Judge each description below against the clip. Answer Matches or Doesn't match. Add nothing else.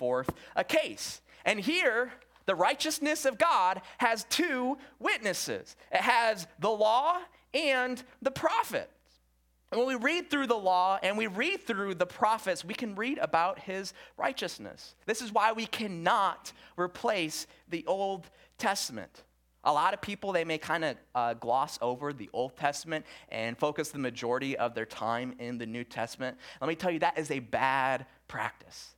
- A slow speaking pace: Doesn't match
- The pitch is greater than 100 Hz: Matches